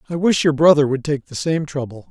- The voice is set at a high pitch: No, medium, 150 Hz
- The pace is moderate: No, fast, 255 wpm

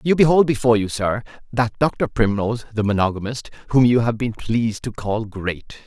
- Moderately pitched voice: No, low, 115 Hz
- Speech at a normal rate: Yes, average, 185 wpm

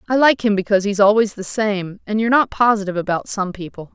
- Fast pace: Yes, fast, 230 wpm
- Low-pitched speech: No, high, 205 Hz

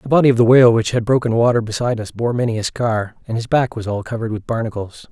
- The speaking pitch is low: Yes, low, 115 Hz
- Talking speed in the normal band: No, fast, 270 wpm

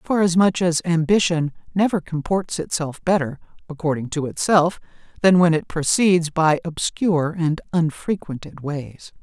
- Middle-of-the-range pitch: Yes, medium, 165 Hz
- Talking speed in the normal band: No, slow, 125 wpm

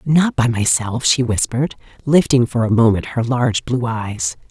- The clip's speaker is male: No, female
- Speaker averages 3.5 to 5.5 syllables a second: Yes, 4.7 syllables/s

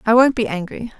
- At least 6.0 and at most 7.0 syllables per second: Yes, 6.1 syllables/s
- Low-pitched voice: No, high, 225 Hz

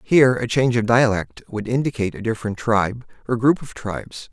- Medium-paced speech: Yes, average, 195 wpm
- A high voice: No, low, 120 Hz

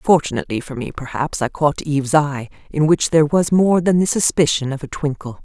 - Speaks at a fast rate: Yes, fast, 210 wpm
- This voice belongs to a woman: Yes, female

